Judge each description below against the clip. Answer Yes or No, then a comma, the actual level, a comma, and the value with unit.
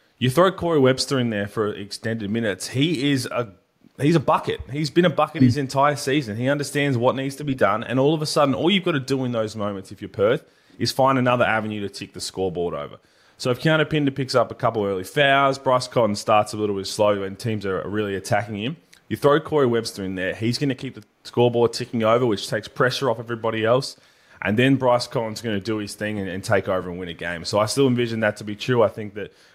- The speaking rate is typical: No, fast, 255 wpm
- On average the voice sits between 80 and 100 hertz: No, low, 120 Hz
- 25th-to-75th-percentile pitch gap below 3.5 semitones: No, average, 4.7 semitones